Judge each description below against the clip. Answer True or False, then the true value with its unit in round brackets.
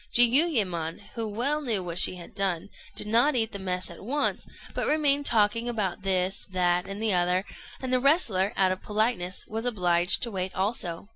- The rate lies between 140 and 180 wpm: False (190 wpm)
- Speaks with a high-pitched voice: True (200 Hz)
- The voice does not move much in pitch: False (4.6 semitones)